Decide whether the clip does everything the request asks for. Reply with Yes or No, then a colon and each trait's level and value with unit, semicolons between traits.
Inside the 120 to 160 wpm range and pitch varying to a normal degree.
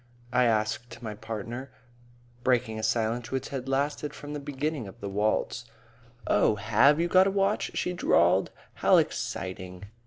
Yes: average, 155 wpm; average, 5.0 semitones